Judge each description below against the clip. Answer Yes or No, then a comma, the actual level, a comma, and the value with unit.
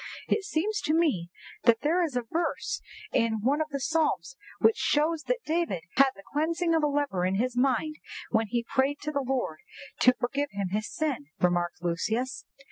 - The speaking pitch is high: Yes, very high, 275 Hz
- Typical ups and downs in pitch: No, wide, 5.9 semitones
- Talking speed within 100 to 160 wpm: No, average, 190 wpm